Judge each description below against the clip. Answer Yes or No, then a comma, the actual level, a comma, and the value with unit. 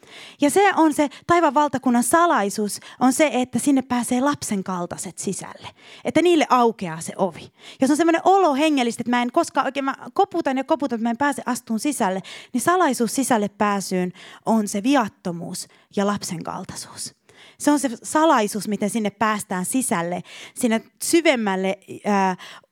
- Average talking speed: No, fast, 165 wpm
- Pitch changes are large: Yes, wide, 6.3 semitones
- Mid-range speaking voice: No, high, 240 Hz